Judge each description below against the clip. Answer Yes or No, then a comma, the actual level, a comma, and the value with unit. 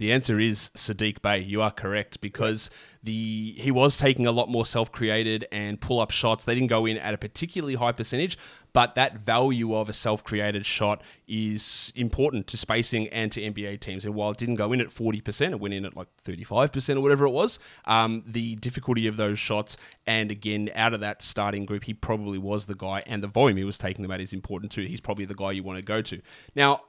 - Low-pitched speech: Yes, low, 110 Hz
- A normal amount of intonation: No, narrow, 2.3 semitones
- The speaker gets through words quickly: Yes, fast, 225 wpm